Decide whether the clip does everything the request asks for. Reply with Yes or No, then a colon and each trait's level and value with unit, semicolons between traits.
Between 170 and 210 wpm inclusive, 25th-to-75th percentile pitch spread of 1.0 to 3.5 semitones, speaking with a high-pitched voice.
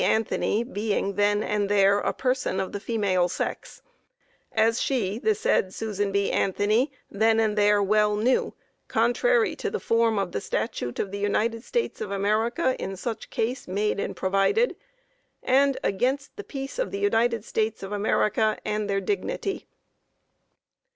No: average, 160 wpm; average, 3.1 semitones; high, 215 Hz